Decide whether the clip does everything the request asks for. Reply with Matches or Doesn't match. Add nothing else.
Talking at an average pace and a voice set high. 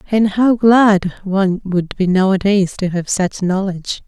Matches